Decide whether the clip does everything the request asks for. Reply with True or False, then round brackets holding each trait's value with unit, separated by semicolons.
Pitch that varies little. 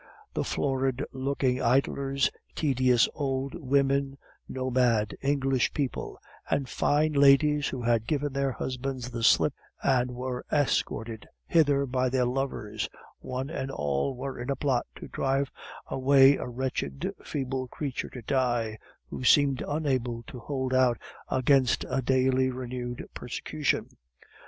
True (1.8 semitones)